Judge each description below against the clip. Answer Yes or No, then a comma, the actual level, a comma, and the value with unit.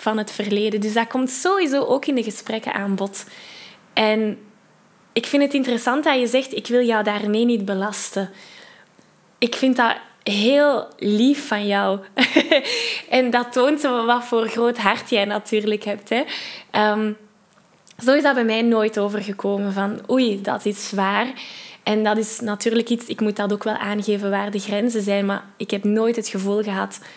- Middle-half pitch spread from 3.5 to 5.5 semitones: No, average, 2.9 semitones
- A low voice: No, high, 215 Hz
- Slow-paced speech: No, average, 175 wpm